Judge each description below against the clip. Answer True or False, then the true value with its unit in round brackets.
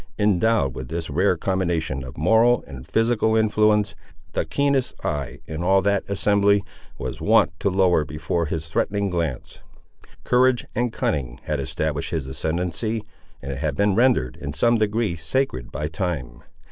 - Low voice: True (90 Hz)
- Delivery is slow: False (155 wpm)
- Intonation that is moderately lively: False (6.1 semitones)